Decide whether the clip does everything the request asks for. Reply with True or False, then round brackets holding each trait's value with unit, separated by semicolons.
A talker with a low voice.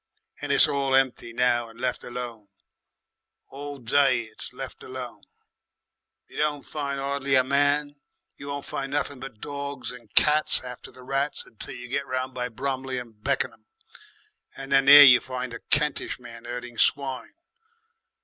True (130 Hz)